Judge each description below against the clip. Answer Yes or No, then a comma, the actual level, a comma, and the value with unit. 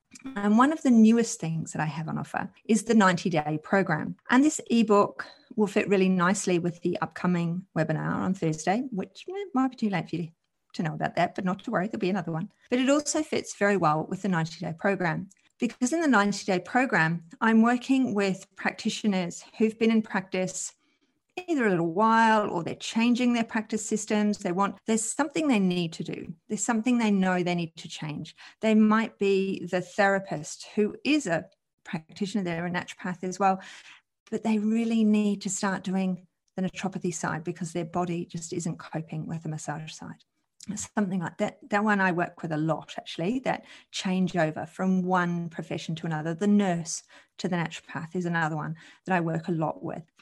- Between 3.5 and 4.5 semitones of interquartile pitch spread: Yes, average, 4.0 semitones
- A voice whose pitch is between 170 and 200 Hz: Yes, high, 190 Hz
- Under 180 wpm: No, average, 195 wpm